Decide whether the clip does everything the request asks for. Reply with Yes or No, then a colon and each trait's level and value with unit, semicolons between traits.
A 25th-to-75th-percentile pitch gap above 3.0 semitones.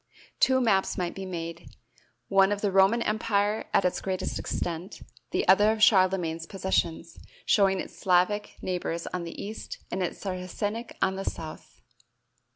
No: narrow, 2.4 semitones